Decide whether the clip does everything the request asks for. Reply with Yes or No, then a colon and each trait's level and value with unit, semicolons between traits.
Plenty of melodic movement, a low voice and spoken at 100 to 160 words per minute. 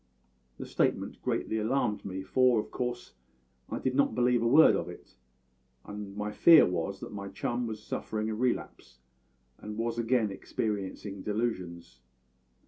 No: average, 3.5 semitones; low, 110 Hz; average, 150 wpm